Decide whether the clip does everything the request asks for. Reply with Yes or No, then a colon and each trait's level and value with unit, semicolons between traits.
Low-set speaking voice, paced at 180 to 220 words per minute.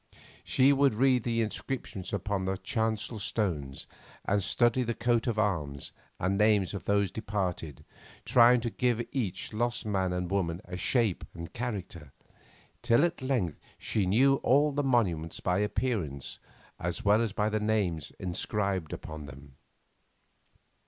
No: low, 105 Hz; average, 150 wpm